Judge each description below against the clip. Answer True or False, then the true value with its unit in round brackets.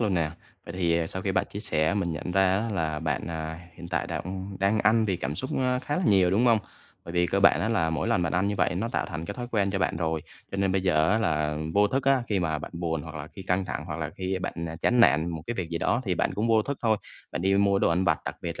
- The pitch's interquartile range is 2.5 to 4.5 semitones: True (3.8 semitones)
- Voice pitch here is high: False (95 Hz)